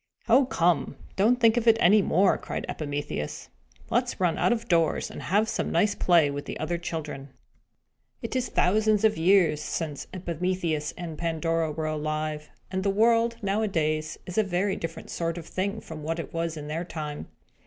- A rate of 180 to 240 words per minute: Yes, average, 185 wpm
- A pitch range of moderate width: Yes, average, 4.5 semitones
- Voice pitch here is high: No, medium, 170 Hz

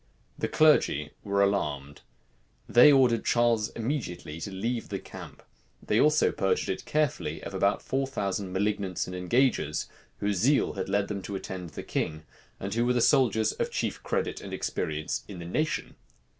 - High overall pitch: No, low, 100 Hz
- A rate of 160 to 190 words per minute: Yes, average, 170 wpm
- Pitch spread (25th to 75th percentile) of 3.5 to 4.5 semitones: No, average, 4.9 semitones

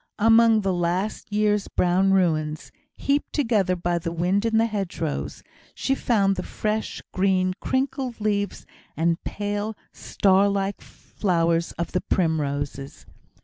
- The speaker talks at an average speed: No, slow, 130 wpm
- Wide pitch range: No, average, 3.8 semitones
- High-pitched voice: Yes, high, 195 Hz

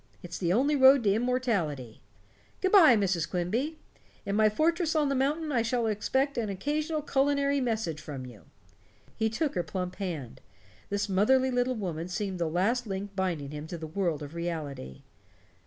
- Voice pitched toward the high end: Yes, high, 205 Hz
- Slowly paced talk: No, average, 170 wpm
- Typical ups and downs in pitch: No, wide, 7.4 semitones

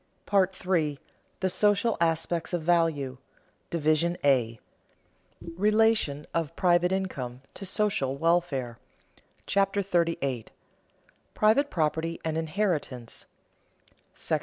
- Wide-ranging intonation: No, average, 4.8 semitones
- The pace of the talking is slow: Yes, slow, 100 wpm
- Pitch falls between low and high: Yes, medium, 170 Hz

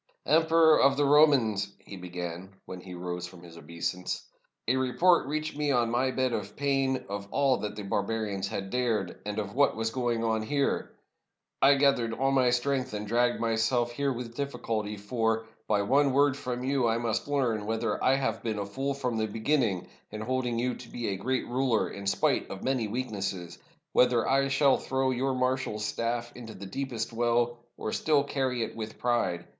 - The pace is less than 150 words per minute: No, average, 195 wpm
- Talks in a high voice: No, low, 120 Hz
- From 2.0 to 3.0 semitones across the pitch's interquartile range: No, average, 4.0 semitones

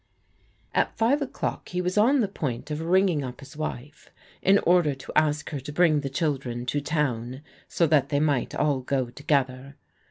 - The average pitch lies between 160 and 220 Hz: No, medium, 150 Hz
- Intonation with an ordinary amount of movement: Yes, average, 4.5 semitones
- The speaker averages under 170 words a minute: No, average, 180 wpm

